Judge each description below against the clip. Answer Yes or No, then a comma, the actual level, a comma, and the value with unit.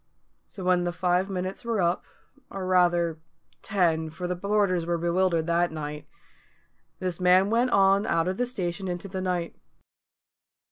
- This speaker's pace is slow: No, average, 155 wpm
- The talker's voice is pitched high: No, medium, 180 Hz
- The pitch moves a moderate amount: No, narrow, 2.0 semitones